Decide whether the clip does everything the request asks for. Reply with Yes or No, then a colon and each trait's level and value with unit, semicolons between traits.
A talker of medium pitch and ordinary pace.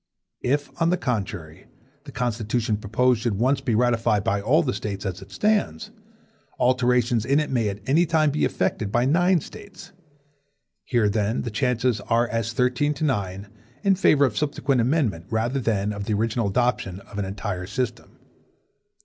No: low, 120 Hz; average, 170 wpm